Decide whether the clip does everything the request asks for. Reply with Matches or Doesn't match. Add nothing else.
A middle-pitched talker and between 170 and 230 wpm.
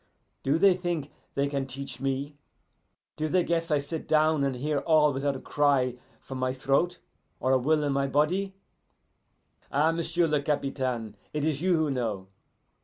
Matches